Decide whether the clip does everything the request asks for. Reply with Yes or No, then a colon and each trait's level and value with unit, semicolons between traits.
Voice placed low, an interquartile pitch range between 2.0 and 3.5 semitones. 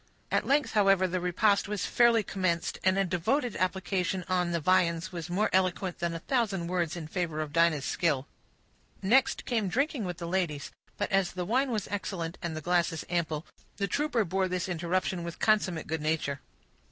No: medium, 180 Hz; average, 2.9 semitones